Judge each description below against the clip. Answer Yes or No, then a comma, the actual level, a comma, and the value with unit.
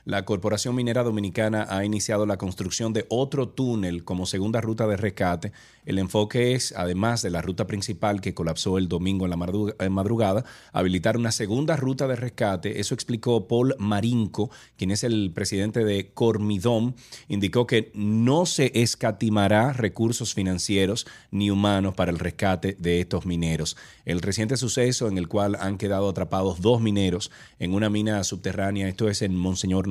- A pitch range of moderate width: Yes, average, 3.3 semitones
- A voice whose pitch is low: Yes, low, 105 Hz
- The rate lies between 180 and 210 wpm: No, average, 165 wpm